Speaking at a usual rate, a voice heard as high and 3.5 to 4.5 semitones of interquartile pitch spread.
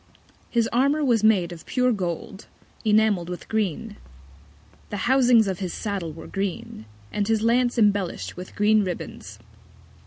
Yes: average, 145 wpm; high, 210 Hz; average, 3.8 semitones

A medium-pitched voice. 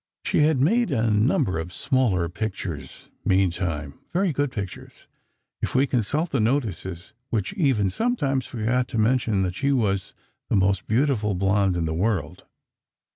No: low, 110 Hz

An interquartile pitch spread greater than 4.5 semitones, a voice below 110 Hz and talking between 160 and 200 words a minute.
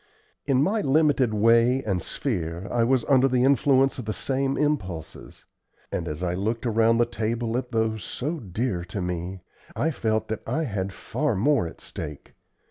No: wide, 5.6 semitones; low, 115 Hz; average, 175 wpm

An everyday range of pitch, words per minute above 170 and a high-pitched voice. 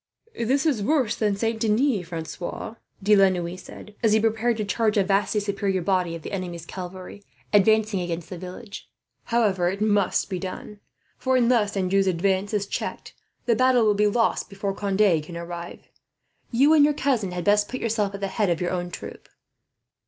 Yes: average, 3.2 semitones; average, 190 wpm; high, 200 Hz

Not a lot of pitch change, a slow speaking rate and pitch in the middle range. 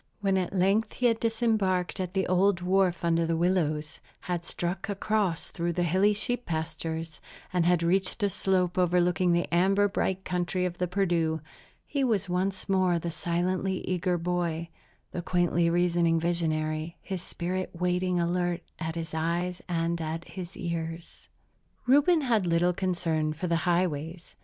No: narrow, 2.0 semitones; average, 155 wpm; medium, 175 Hz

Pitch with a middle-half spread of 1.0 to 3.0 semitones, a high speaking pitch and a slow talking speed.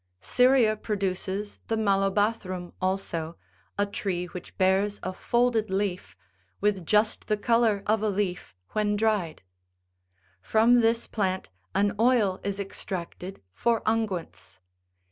Yes: average, 2.7 semitones; high, 205 Hz; slow, 120 wpm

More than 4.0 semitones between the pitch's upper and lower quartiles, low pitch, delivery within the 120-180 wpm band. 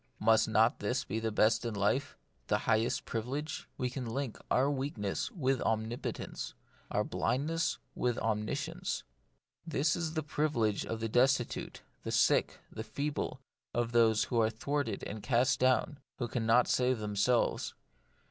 No: average, 3.7 semitones; low, 120 Hz; average, 145 wpm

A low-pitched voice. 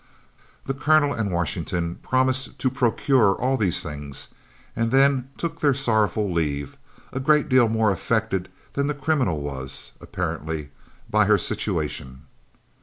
Yes: low, 110 Hz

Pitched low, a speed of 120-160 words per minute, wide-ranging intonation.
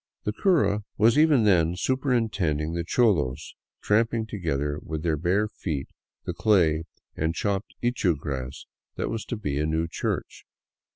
Yes: very low, 90 Hz; average, 155 wpm; wide, 6.1 semitones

